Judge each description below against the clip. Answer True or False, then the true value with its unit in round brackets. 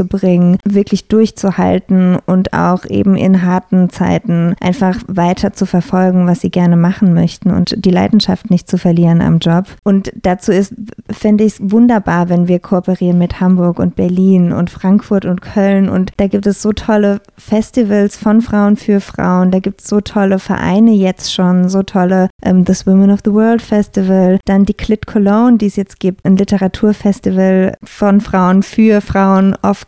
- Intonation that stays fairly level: True (1.9 semitones)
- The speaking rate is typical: True (175 wpm)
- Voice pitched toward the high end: True (195 Hz)